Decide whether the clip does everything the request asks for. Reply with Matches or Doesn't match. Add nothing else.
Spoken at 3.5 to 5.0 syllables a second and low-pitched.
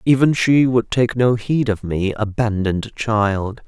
Matches